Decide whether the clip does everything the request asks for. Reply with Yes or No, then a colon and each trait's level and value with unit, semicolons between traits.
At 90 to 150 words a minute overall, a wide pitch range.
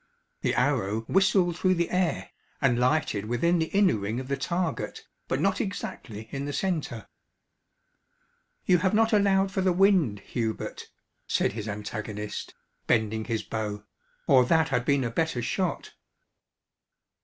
Yes: average, 145 wpm; wide, 8.8 semitones